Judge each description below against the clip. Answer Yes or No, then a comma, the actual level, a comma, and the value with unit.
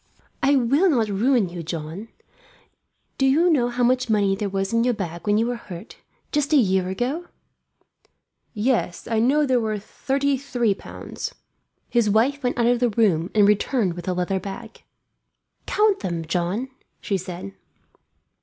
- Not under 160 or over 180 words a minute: Yes, average, 170 wpm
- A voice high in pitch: Yes, high, 225 Hz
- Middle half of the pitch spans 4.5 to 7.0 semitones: Yes, average, 5.0 semitones